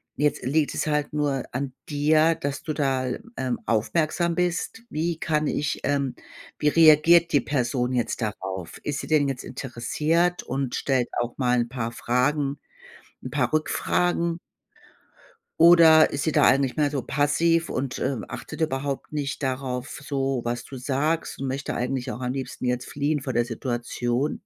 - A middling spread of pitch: Yes, average, 3.4 semitones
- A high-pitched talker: No, medium, 140 Hz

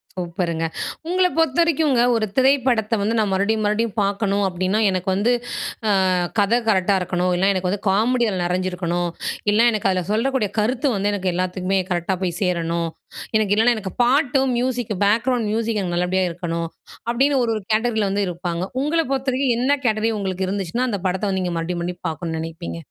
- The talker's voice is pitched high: Yes, high, 205 Hz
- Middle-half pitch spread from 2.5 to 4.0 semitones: No, average, 4.7 semitones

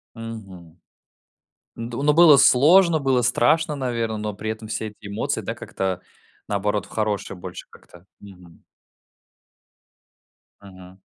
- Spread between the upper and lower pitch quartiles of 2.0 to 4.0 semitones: No, average, 4.4 semitones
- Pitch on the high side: No, low, 110 Hz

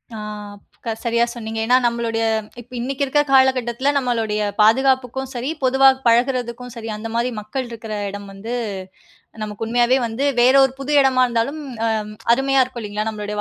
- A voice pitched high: Yes, high, 240 Hz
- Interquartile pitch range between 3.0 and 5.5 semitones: No, narrow, 2.6 semitones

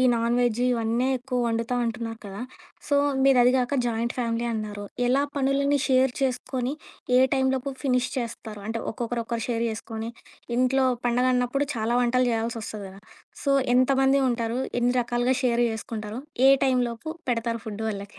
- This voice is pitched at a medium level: No, high, 240 Hz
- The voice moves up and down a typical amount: No, narrow, 2.1 semitones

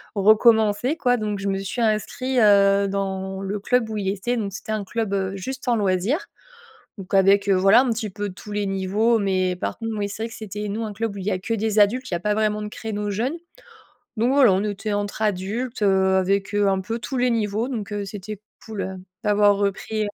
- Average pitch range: No, narrow, 2.2 semitones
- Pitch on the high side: Yes, high, 205 Hz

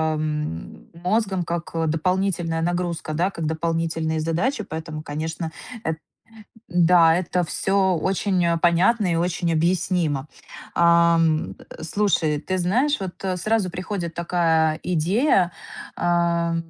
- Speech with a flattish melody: Yes, narrow, 2.1 semitones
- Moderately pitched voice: Yes, medium, 170 Hz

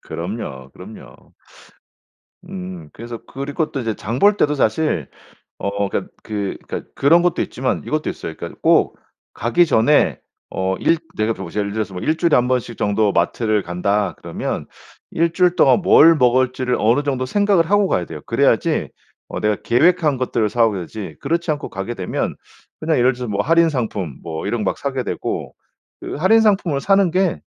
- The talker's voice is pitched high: No, low, 125 Hz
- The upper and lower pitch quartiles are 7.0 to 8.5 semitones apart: Yes, wide, 7.7 semitones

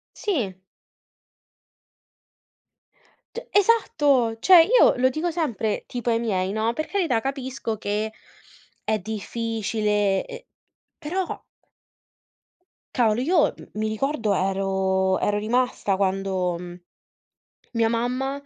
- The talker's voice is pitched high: Yes, high, 225 Hz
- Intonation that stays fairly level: No, average, 5.1 semitones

